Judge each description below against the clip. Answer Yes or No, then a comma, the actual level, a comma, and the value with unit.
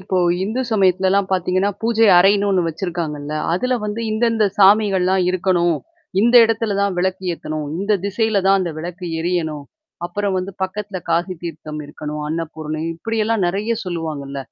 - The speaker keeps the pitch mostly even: No, average, 3.6 semitones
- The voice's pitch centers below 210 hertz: Yes, medium, 185 Hz